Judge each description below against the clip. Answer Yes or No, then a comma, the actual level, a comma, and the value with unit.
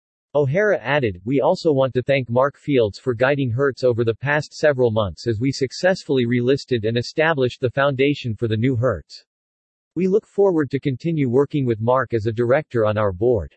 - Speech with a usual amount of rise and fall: Yes, average, 3.4 semitones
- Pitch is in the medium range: No, low, 130 Hz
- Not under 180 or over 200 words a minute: Yes, average, 190 wpm